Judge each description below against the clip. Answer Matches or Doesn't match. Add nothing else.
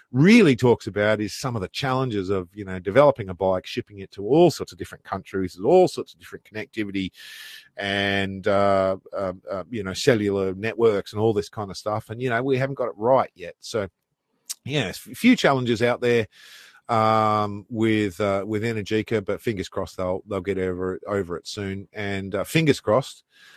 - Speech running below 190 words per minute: Doesn't match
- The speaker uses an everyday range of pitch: Matches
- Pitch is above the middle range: Doesn't match